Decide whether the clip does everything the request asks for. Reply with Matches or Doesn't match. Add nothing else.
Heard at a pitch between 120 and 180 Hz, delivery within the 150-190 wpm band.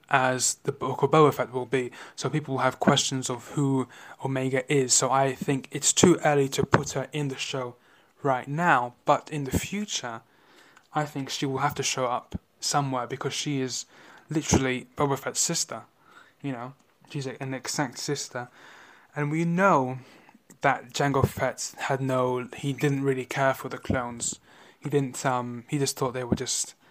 Matches